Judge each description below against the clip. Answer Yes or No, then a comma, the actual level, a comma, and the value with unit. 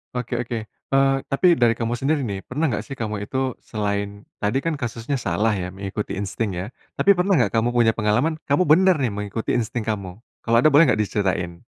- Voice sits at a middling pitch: No, low, 115 Hz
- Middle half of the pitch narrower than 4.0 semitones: No, average, 4.6 semitones